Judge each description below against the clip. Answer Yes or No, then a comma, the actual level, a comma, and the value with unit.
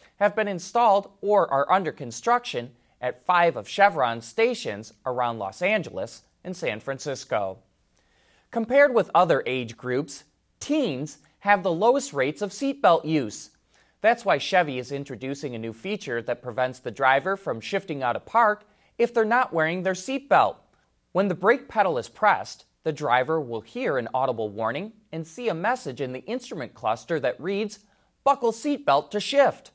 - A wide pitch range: Yes, wide, 8.8 semitones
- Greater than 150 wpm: Yes, average, 165 wpm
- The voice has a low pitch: No, medium, 160 Hz